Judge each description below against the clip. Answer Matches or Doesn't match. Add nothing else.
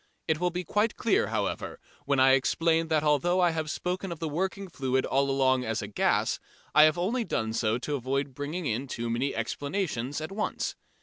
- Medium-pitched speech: Matches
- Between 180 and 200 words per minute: Matches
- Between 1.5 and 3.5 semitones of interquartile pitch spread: Doesn't match